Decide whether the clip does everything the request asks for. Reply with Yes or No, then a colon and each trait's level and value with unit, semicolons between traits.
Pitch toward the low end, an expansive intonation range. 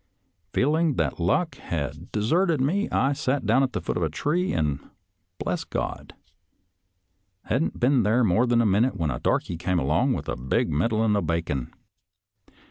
Yes: low, 110 Hz; wide, 8.3 semitones